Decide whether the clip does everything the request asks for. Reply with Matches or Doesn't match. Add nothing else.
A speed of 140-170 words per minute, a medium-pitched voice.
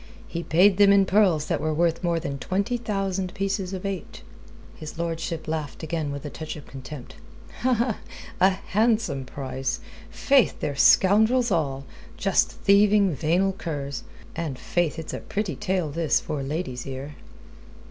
Matches